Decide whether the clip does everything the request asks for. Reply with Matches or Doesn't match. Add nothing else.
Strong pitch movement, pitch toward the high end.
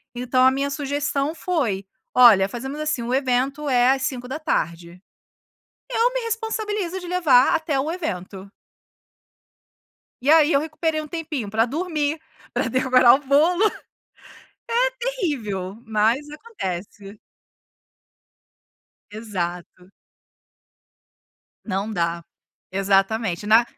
Matches